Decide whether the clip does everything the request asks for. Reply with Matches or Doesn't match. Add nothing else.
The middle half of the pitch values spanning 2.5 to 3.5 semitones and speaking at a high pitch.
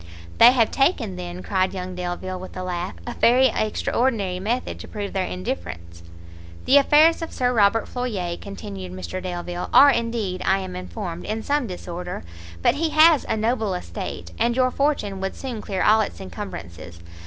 Doesn't match